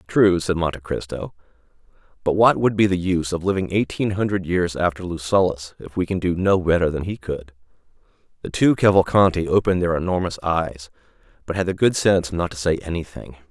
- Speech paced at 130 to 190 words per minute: Yes, average, 185 wpm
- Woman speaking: No, male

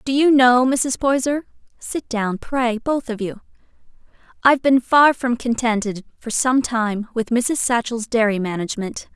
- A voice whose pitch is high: Yes, high, 240 Hz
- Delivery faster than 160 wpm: No, average, 145 wpm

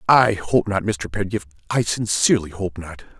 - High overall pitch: No, very low, 95 Hz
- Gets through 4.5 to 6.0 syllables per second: Yes, 4.8 syllables/s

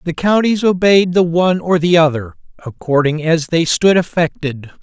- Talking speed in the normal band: Yes, average, 160 wpm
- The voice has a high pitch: No, medium, 170 Hz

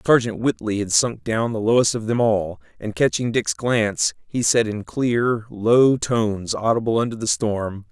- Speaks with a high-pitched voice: No, low, 110 Hz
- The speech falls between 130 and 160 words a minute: No, average, 180 wpm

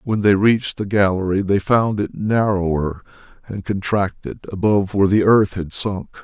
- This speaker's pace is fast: No, average, 165 wpm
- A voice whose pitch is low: Yes, low, 100 Hz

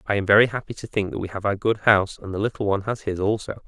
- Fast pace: Yes, fast, 310 wpm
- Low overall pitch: Yes, low, 105 Hz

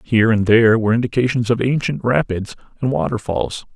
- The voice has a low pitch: Yes, low, 115 Hz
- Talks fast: No, average, 160 wpm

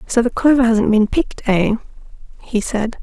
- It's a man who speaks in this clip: No, female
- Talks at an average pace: Yes, average, 180 wpm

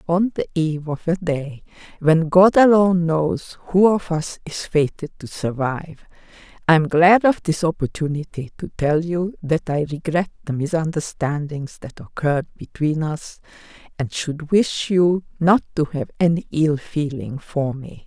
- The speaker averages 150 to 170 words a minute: Yes, average, 155 wpm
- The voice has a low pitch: No, medium, 160 Hz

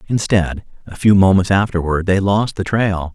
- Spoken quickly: No, average, 170 wpm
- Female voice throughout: No, male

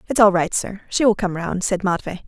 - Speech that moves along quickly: Yes, fast, 265 wpm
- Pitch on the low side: No, high, 190 Hz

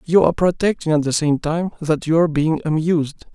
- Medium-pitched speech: Yes, medium, 160 Hz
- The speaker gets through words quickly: Yes, fast, 215 wpm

